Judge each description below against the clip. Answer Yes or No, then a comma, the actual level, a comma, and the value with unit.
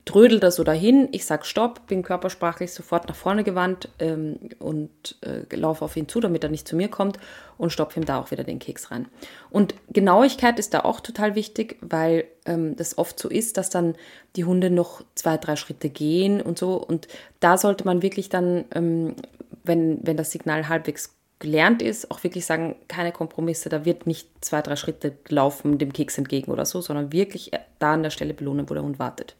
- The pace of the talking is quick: Yes, fast, 205 wpm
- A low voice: No, medium, 170 Hz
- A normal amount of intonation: Yes, average, 3.5 semitones